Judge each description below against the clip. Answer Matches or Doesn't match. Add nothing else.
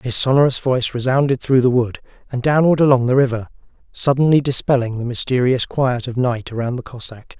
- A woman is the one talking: Doesn't match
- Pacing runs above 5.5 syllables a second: Matches